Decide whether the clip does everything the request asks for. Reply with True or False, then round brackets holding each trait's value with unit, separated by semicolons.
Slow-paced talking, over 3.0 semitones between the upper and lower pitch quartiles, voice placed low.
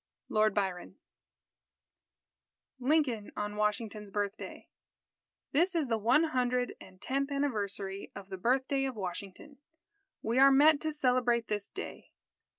False (130 wpm; 5.1 semitones; 235 Hz)